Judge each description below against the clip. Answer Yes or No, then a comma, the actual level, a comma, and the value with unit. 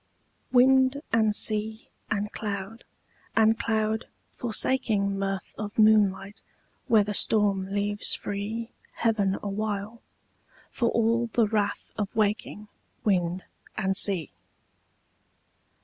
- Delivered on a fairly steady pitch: Yes, narrow, 2.0 semitones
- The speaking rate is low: Yes, slow, 100 wpm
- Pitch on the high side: Yes, high, 210 Hz